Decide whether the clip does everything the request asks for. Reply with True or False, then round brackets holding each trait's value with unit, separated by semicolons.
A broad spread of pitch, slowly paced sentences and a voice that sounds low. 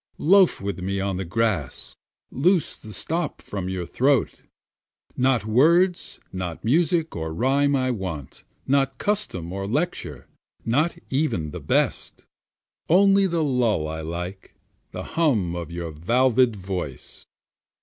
True (8.7 semitones; 130 wpm; 115 Hz)